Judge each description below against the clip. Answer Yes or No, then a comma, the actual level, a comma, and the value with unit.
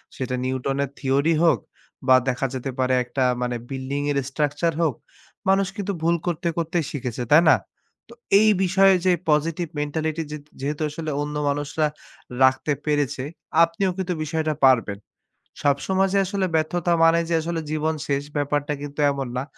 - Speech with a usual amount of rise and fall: Yes, average, 3.4 semitones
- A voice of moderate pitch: Yes, medium, 150 Hz